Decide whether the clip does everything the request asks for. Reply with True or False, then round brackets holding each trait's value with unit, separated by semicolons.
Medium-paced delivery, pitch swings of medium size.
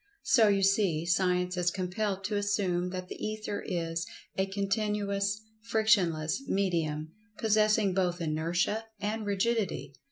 False (125 wpm; 3.0 semitones)